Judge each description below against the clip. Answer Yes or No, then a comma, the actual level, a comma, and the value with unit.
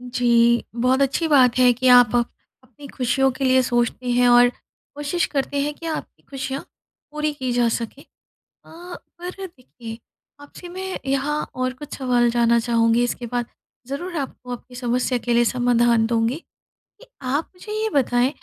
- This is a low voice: No, very high, 255 Hz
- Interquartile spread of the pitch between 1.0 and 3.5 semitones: Yes, average, 2.8 semitones